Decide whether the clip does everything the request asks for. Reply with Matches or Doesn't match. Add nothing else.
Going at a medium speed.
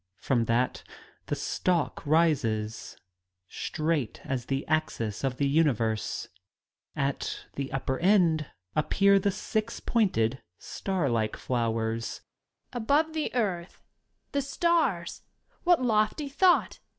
Doesn't match